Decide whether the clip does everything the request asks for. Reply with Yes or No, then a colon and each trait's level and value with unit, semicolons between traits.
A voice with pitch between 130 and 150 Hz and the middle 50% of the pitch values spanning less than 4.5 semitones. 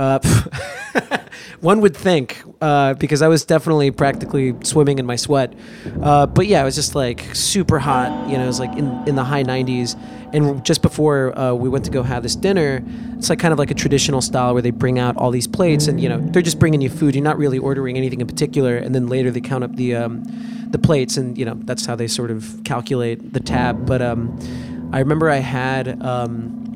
Yes: low, 135 Hz; average, 3.3 semitones